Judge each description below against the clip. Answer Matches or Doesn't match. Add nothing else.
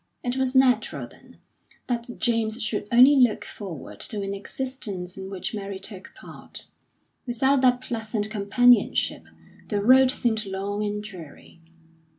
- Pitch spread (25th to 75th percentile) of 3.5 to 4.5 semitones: Matches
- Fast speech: Doesn't match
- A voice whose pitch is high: Matches